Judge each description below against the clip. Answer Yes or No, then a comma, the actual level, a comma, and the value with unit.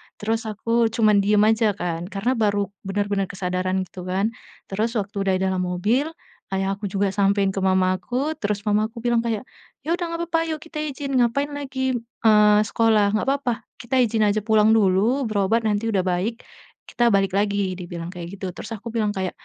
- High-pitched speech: Yes, high, 210 Hz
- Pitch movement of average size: Yes, average, 3.3 semitones